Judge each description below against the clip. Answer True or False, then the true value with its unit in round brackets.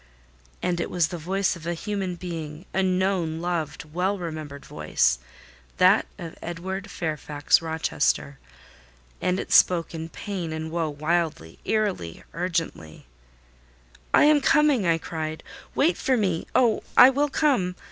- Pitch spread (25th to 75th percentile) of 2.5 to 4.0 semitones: True (3.3 semitones)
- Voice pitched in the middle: True (170 Hz)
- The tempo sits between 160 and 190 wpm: False (135 wpm)